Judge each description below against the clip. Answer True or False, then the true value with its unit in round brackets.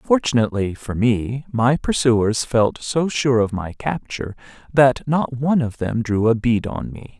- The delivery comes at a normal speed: True (175 wpm)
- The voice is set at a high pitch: False (120 Hz)